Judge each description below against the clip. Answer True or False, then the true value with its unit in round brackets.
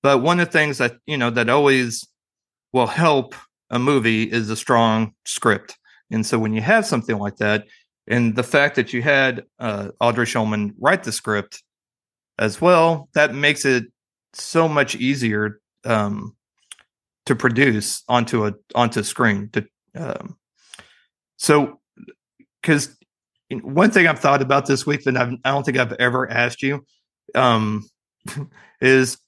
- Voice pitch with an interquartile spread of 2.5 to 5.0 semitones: True (4.0 semitones)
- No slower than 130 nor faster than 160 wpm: True (155 wpm)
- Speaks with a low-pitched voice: True (125 Hz)